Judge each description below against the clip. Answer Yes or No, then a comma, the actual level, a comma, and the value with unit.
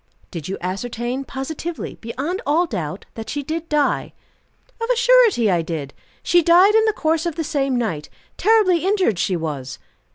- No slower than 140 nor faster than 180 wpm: Yes, average, 170 wpm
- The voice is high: Yes, very high, 285 Hz